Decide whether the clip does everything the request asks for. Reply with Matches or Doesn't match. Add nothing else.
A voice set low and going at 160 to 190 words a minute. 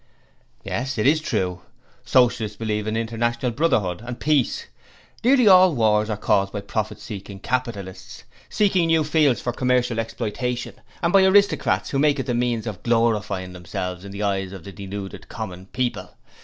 Matches